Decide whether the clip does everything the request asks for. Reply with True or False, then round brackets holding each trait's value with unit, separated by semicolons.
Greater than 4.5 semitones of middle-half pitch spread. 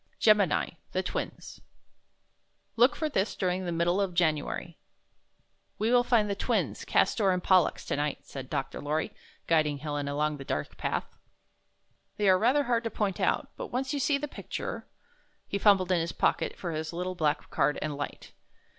True (5.6 semitones)